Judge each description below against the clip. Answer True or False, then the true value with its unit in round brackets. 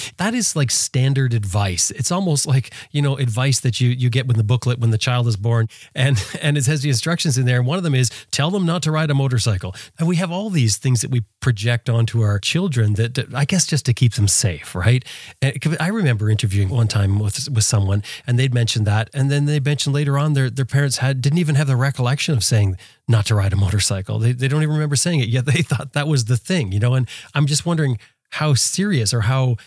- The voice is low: True (130 Hz)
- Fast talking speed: True (250 wpm)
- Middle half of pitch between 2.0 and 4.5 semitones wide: True (4.0 semitones)